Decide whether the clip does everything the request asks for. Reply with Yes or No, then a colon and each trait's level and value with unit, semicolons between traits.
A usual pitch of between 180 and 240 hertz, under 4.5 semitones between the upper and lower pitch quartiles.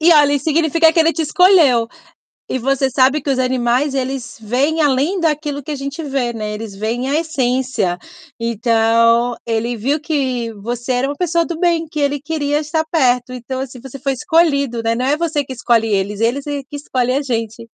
No: very high, 265 Hz; average, 4.0 semitones